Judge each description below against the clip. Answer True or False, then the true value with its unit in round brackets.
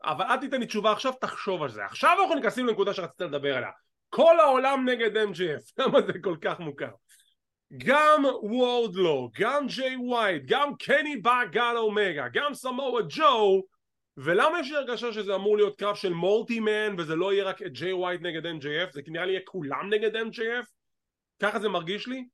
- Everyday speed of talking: True (180 wpm)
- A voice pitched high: True (220 Hz)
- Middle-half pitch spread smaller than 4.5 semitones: False (5.3 semitones)